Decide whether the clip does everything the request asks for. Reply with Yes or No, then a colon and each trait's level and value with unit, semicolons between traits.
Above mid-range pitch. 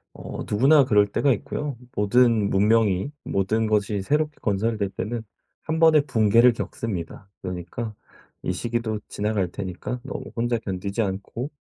No: low, 110 Hz